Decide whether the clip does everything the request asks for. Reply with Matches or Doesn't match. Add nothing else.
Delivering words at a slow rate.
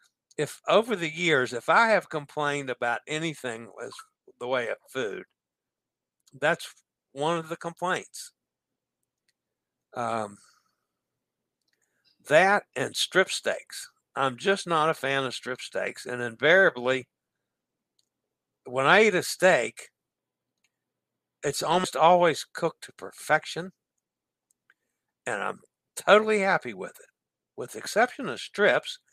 Matches